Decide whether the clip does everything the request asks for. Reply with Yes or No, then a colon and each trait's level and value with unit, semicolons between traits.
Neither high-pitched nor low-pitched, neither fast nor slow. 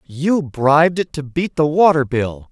Yes: medium, 150 Hz; average, 190 wpm